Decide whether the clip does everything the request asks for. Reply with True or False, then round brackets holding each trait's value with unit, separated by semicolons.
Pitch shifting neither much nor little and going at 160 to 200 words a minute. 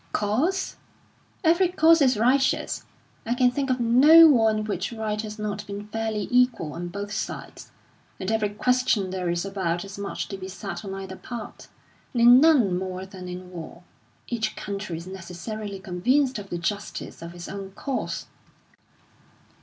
True (4.5 semitones; 170 wpm)